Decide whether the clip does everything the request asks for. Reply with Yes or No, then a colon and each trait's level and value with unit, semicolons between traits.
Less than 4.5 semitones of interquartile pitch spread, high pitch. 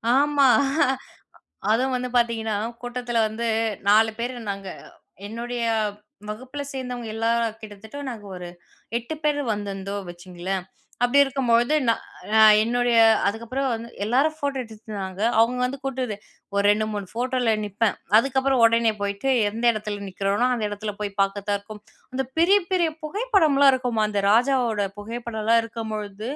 Yes: average, 3.4 semitones; high, 230 Hz